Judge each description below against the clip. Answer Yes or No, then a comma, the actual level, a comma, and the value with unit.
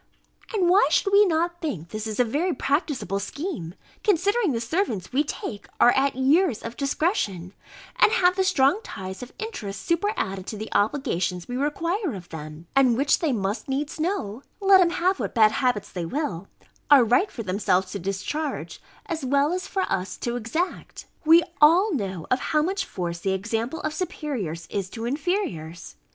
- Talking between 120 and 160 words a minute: No, average, 175 wpm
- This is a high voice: Yes, very high, 270 Hz